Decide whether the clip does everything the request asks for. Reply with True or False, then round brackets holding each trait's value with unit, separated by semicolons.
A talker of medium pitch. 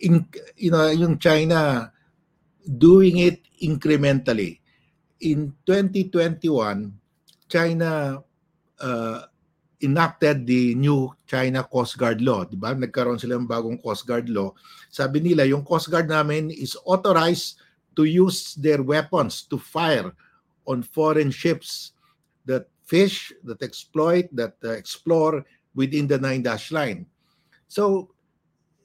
True (155 Hz)